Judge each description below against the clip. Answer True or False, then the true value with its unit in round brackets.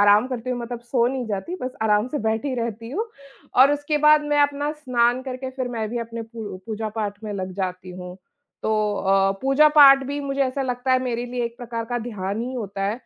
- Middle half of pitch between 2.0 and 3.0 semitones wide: False (3.6 semitones)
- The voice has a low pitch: False (240 Hz)